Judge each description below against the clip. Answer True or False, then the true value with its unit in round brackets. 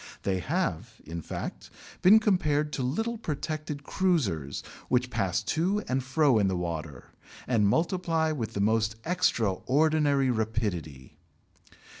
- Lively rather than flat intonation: True (8.0 semitones)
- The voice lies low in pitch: True (130 Hz)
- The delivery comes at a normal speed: False (125 wpm)